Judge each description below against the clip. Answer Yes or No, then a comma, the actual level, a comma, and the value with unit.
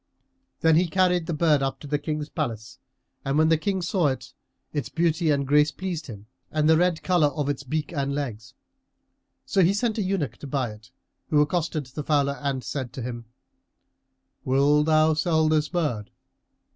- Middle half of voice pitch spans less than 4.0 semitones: Yes, average, 3.1 semitones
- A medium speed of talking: Yes, average, 185 wpm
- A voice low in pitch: No, medium, 150 Hz